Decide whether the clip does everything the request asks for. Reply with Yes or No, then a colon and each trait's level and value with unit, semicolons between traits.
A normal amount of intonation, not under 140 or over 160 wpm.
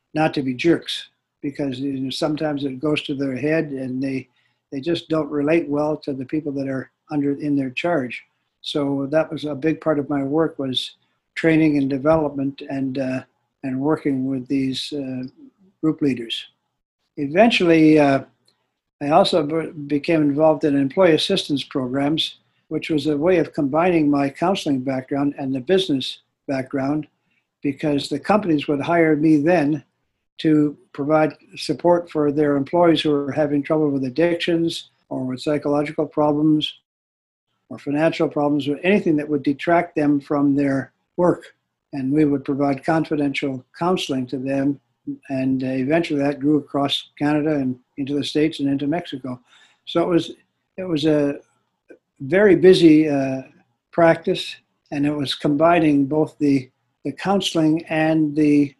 No: narrow, 2.2 semitones; average, 155 wpm